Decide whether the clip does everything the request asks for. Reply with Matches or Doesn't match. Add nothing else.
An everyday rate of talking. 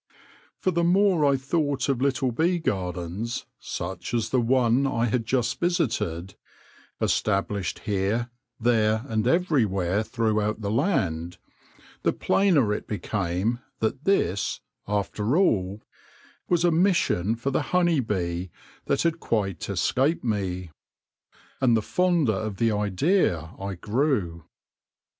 Doesn't match